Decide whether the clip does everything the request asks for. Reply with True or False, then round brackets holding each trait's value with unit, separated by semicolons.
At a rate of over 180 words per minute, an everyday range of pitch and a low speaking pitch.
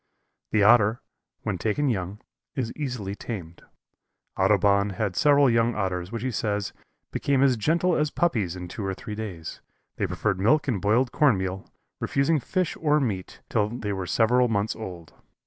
False (165 wpm; 5.0 semitones; 110 Hz)